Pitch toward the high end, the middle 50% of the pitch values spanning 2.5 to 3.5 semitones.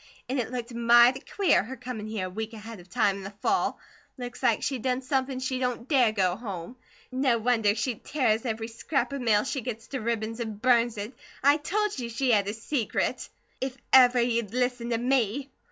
Yes: high, 240 Hz; average, 2.8 semitones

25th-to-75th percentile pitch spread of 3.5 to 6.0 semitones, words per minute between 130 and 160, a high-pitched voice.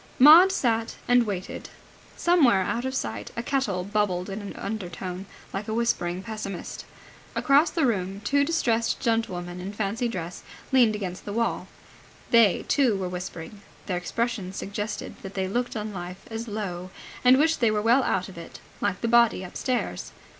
No: average, 4.2 semitones; average, 170 wpm; high, 210 Hz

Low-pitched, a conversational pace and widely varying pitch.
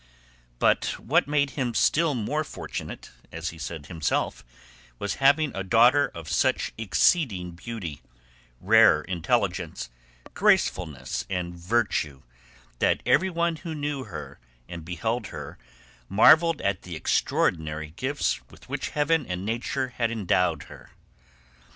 No: low, 110 Hz; slow, 125 wpm; wide, 8.7 semitones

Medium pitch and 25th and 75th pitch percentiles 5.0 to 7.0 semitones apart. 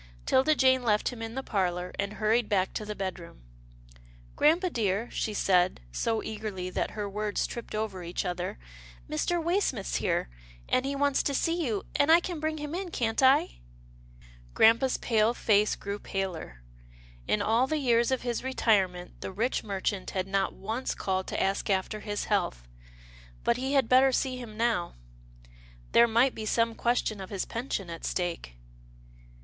No: high, 215 Hz; average, 5.3 semitones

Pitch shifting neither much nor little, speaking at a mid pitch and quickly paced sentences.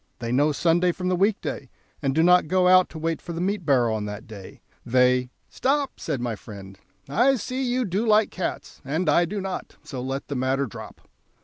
No: wide, 6.7 semitones; medium, 160 Hz; fast, 220 wpm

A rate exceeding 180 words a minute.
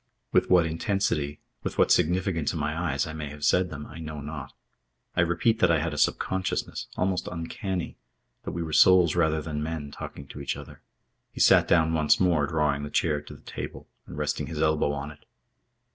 Yes: fast, 205 wpm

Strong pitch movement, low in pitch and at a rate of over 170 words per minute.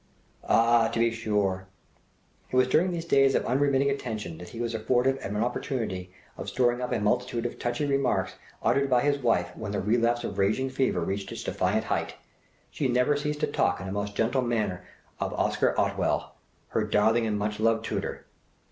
No: average, 4.1 semitones; low, 115 Hz; average, 190 wpm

